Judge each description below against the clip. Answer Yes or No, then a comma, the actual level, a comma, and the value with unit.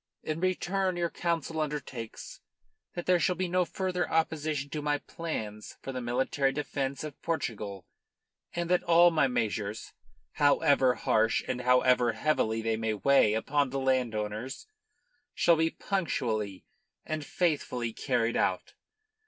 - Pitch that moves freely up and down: Yes, wide, 5.9 semitones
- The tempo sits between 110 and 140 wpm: Yes, slow, 135 wpm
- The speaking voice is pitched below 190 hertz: Yes, medium, 140 Hz